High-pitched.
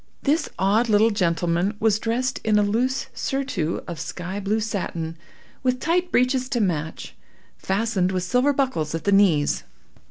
Yes: high, 210 Hz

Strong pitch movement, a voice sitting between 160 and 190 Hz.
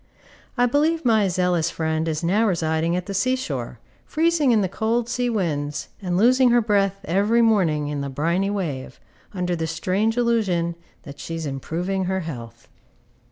Yes: wide, 5.7 semitones; medium, 185 Hz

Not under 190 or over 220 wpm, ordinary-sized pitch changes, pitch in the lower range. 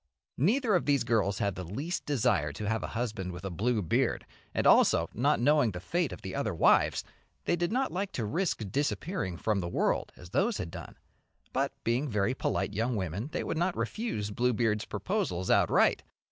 No: average, 195 wpm; wide, 7.7 semitones; low, 115 Hz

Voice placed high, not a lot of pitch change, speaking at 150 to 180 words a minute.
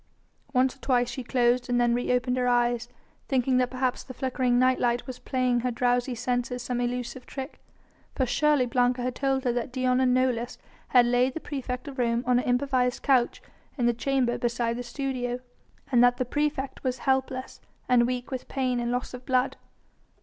No: very high, 250 Hz; narrow, 1.1 semitones; average, 195 wpm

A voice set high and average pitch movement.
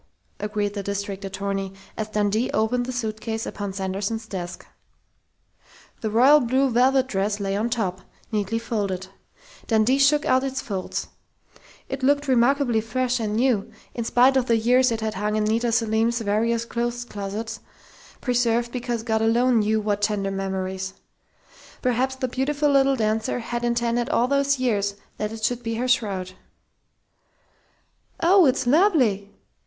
Yes: high, 225 Hz; average, 3.2 semitones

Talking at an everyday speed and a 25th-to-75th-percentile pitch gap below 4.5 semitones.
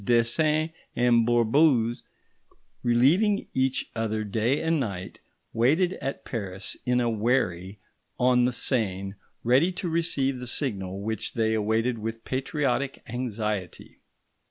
No: slow, 120 wpm; average, 3.6 semitones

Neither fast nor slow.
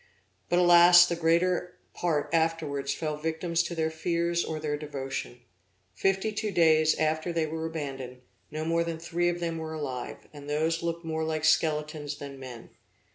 Yes: average, 170 wpm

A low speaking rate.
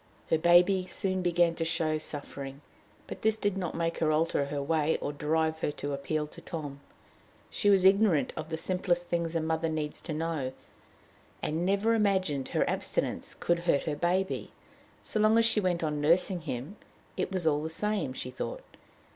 No: average, 185 wpm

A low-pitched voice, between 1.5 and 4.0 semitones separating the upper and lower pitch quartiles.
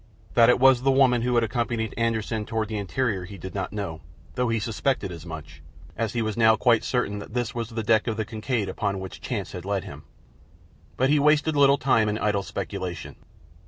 Yes: low, 110 Hz; average, 3.3 semitones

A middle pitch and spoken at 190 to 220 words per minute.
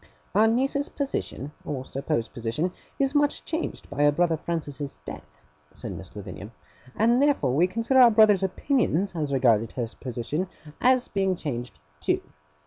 No: medium, 165 Hz; average, 150 wpm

